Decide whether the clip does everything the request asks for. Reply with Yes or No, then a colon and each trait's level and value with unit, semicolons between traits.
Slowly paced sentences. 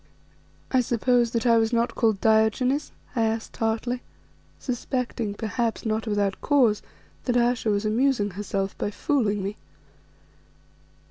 Yes: slow, 130 wpm